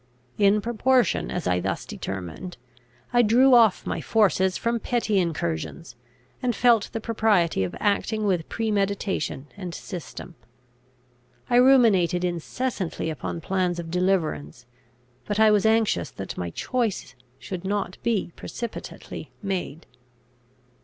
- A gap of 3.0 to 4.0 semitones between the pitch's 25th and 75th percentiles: No, average, 4.7 semitones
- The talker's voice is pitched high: Yes, high, 195 Hz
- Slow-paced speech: Yes, slow, 125 wpm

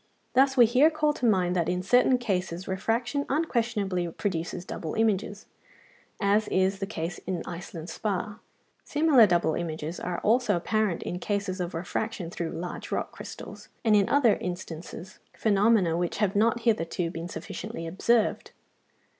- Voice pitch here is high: Yes, high, 195 Hz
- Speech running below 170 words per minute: Yes, average, 150 wpm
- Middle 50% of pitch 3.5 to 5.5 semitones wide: Yes, average, 4.4 semitones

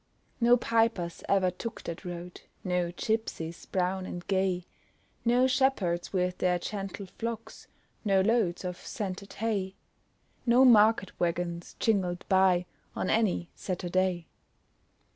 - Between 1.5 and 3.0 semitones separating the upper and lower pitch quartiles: No, average, 3.9 semitones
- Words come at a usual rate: No, slow, 120 wpm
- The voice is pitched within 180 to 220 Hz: Yes, high, 190 Hz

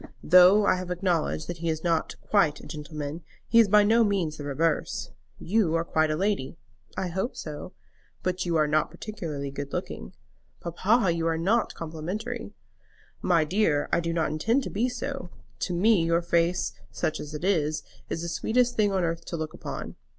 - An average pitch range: Yes, average, 4.2 semitones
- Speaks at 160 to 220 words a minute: Yes, average, 190 wpm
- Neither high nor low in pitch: Yes, medium, 170 Hz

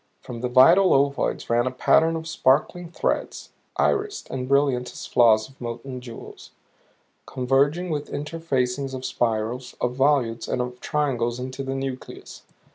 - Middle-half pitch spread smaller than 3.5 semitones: Yes, average, 2.7 semitones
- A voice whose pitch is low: Yes, low, 130 Hz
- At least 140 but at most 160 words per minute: Yes, average, 145 wpm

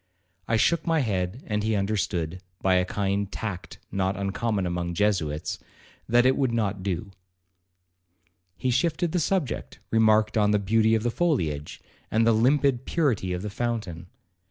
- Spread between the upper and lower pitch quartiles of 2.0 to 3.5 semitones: No, average, 4.3 semitones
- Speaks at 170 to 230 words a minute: No, average, 160 wpm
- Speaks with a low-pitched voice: Yes, low, 105 Hz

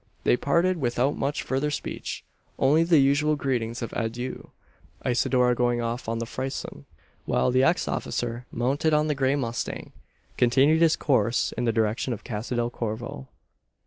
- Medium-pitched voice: No, low, 125 Hz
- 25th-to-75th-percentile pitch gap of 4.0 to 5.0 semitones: No, average, 3.2 semitones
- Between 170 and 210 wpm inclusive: No, average, 160 wpm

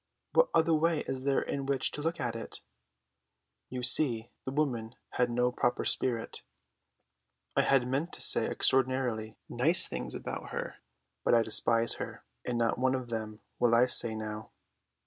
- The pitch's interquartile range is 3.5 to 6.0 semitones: No, average, 2.9 semitones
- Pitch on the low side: Yes, low, 125 Hz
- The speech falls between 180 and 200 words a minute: No, average, 165 wpm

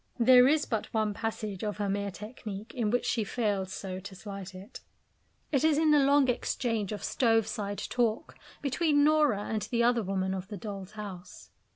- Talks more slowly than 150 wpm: No, average, 190 wpm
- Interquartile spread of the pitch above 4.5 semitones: No, average, 3.8 semitones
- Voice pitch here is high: Yes, high, 215 Hz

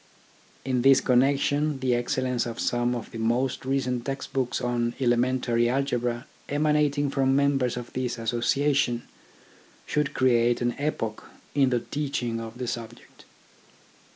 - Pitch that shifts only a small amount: Yes, narrow, 2.3 semitones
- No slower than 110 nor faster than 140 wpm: Yes, slow, 135 wpm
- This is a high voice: No, low, 125 Hz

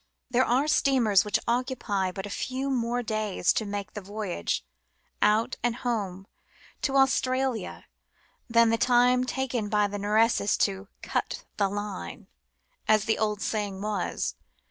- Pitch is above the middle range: Yes, high, 215 Hz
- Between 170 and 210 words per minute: No, average, 145 wpm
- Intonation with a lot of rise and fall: No, average, 3.2 semitones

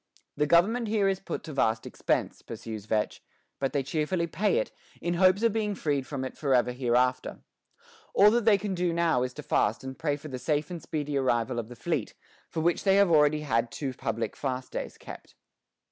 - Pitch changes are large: Yes, wide, 6.0 semitones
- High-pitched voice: No, medium, 150 Hz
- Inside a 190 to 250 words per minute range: Yes, fast, 205 wpm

